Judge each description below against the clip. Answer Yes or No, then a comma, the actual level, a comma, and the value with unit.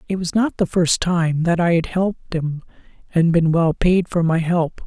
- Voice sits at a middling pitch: Yes, medium, 170 Hz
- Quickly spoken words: Yes, fast, 220 wpm